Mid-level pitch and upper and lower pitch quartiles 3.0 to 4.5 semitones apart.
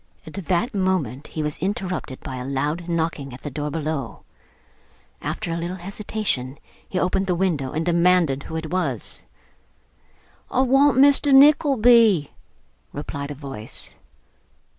No: medium, 170 Hz; wide, 5.4 semitones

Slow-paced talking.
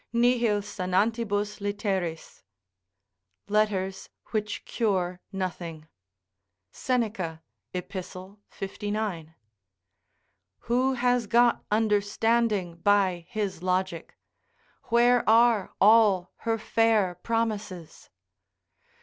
Yes: slow, 75 wpm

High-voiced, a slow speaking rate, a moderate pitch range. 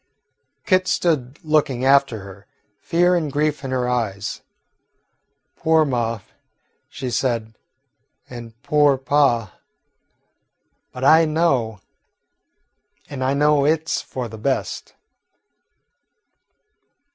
No: low, 135 Hz; slow, 100 wpm; average, 4.3 semitones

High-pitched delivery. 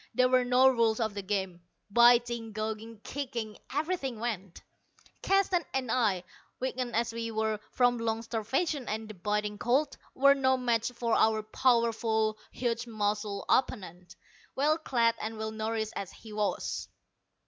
Yes: high, 230 Hz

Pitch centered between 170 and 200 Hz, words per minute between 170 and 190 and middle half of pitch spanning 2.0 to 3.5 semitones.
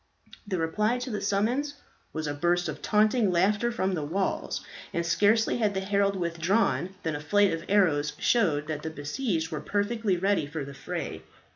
No: high, 190 Hz; average, 180 wpm; average, 4.5 semitones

